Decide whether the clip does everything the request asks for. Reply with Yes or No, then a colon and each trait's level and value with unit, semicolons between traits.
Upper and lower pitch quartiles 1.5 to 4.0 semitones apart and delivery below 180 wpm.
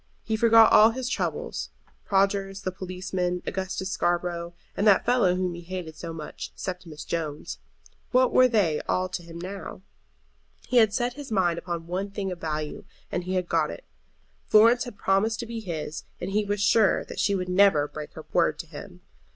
No: average, 3.5 semitones; average, 190 wpm